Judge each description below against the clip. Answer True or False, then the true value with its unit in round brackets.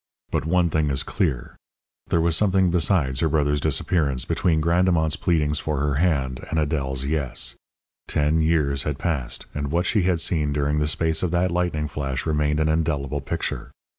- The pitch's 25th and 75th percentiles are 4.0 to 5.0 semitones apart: False (2.8 semitones)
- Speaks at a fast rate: False (175 wpm)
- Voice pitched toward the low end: True (75 Hz)